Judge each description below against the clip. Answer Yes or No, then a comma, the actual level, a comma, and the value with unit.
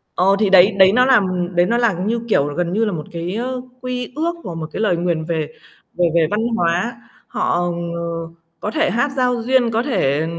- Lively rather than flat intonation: Yes, wide, 6.0 semitones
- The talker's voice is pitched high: Yes, high, 210 Hz